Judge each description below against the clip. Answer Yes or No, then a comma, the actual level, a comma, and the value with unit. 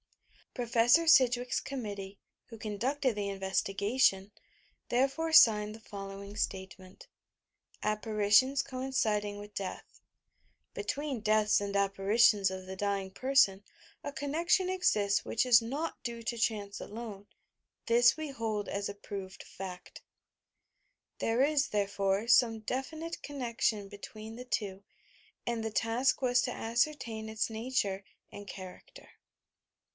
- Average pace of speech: No, slow, 120 wpm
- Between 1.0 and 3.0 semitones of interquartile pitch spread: No, average, 4.0 semitones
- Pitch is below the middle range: No, high, 220 Hz